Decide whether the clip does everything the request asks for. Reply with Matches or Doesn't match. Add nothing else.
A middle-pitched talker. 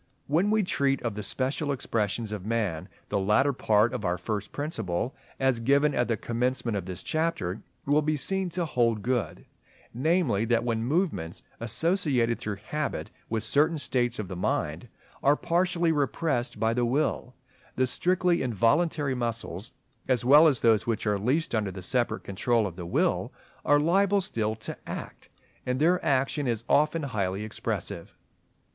Doesn't match